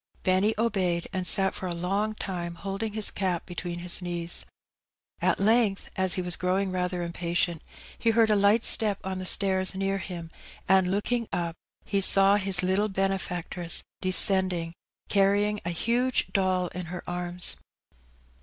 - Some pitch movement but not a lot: No, narrow, 2.2 semitones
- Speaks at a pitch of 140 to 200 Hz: Yes, high, 190 Hz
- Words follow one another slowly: No, average, 160 wpm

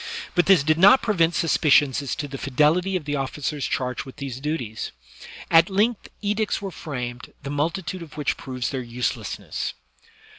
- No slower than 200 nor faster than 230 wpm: No, average, 170 wpm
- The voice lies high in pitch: No, medium, 150 Hz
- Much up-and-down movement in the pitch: No, average, 5.0 semitones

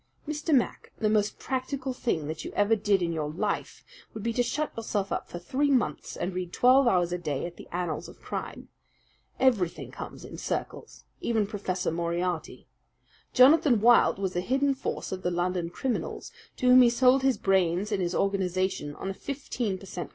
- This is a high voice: Yes, high, 200 Hz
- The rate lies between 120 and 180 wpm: No, average, 190 wpm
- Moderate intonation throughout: No, wide, 6.1 semitones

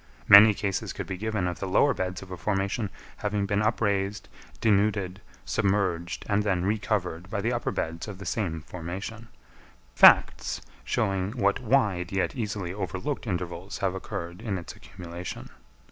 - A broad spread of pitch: No, narrow, 2.6 semitones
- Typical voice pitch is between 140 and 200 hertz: No, low, 100 Hz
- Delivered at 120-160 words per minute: Yes, average, 155 wpm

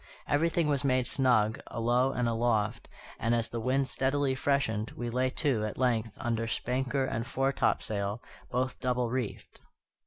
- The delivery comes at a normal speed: Yes, average, 150 wpm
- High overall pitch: No, low, 125 Hz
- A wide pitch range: No, average, 2.7 semitones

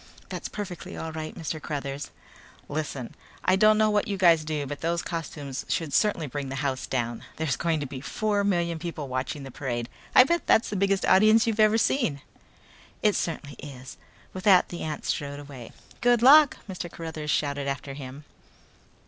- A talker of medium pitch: Yes, medium, 160 Hz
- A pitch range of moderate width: No, wide, 5.8 semitones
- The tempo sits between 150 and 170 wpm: No, average, 180 wpm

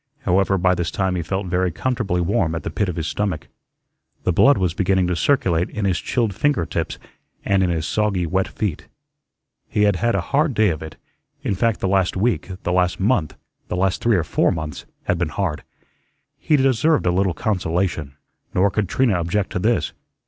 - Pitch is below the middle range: Yes, very low, 95 Hz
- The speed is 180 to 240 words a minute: Yes, average, 200 wpm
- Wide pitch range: No, average, 3.3 semitones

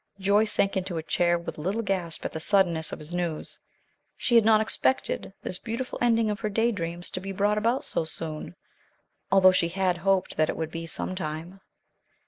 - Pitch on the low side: No, medium, 185 Hz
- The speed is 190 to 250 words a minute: Yes, average, 200 wpm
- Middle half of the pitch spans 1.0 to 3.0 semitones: No, average, 4.0 semitones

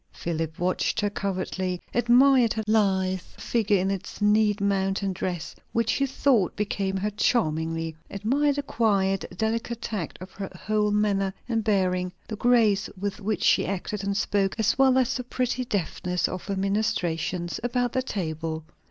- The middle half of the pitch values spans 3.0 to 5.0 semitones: Yes, average, 3.3 semitones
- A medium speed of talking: Yes, average, 160 wpm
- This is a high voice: Yes, high, 200 Hz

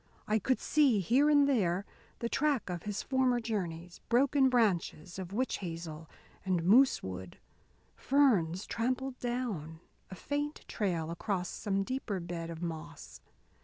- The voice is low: No, high, 200 Hz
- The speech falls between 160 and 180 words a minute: No, average, 140 wpm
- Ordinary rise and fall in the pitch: No, wide, 7.0 semitones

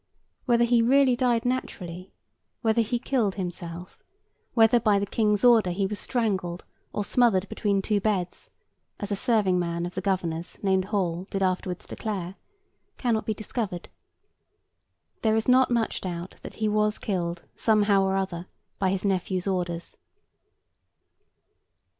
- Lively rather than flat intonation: No, average, 3.5 semitones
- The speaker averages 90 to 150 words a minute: Yes, average, 145 wpm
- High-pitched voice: Yes, high, 200 Hz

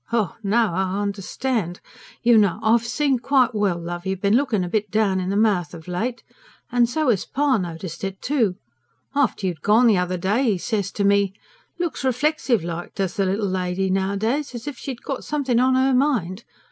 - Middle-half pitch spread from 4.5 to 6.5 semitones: Yes, average, 4.9 semitones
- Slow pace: No, average, 195 wpm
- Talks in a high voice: Yes, high, 210 Hz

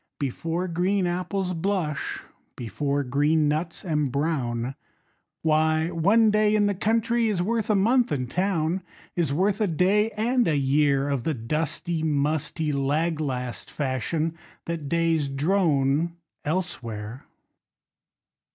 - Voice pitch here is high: No, medium, 160 Hz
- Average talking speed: No, slow, 125 wpm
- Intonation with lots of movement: No, average, 4.8 semitones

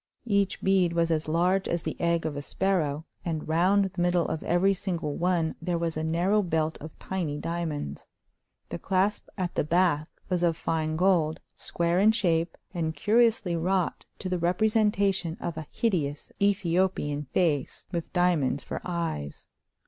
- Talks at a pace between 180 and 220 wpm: No, average, 165 wpm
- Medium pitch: Yes, medium, 170 Hz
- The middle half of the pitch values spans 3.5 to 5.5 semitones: No, average, 2.9 semitones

